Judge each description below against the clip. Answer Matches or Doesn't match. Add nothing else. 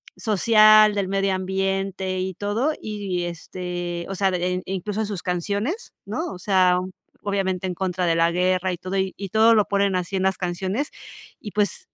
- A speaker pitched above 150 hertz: Matches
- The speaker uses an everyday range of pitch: Doesn't match